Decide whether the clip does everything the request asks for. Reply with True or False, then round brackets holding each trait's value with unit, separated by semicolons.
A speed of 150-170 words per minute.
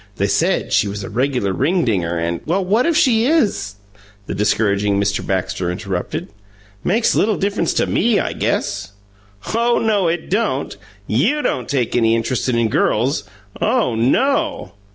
True (155 wpm)